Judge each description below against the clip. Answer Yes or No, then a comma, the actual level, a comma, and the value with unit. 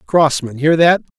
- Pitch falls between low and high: Yes, medium, 155 Hz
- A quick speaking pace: No, average, 150 wpm